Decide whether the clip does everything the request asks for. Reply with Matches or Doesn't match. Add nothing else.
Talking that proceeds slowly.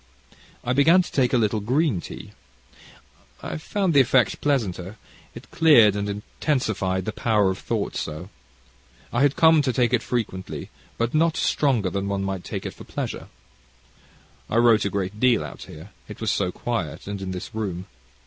Doesn't match